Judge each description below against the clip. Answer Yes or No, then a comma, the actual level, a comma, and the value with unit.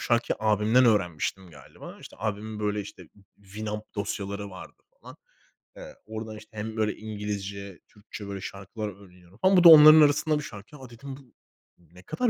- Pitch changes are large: No, average, 3.0 semitones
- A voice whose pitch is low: Yes, low, 105 Hz